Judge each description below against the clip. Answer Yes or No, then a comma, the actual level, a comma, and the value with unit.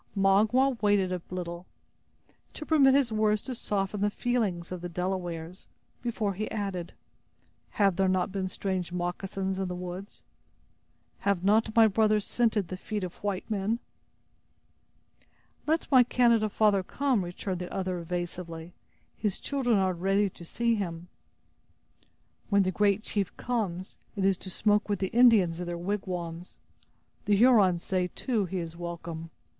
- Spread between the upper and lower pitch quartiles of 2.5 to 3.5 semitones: Yes, average, 3.2 semitones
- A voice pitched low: No, high, 195 Hz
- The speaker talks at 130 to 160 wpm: Yes, average, 150 wpm